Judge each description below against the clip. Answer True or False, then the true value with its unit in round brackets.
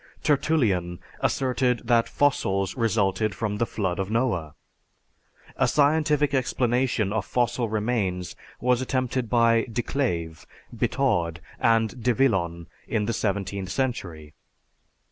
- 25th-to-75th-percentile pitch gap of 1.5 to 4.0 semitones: False (4.7 semitones)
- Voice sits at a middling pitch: False (115 Hz)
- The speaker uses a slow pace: True (115 wpm)